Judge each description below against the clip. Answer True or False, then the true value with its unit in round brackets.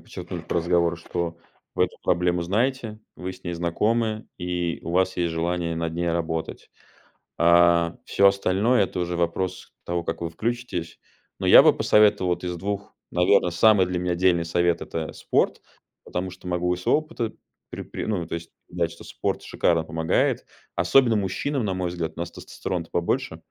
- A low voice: True (90 Hz)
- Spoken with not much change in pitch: True (2.1 semitones)